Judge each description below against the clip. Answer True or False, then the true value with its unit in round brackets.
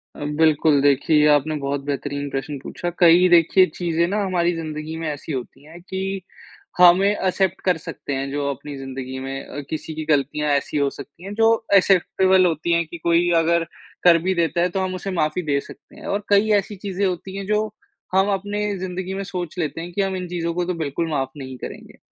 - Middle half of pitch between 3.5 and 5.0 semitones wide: True (4.1 semitones)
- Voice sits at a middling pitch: True (170 Hz)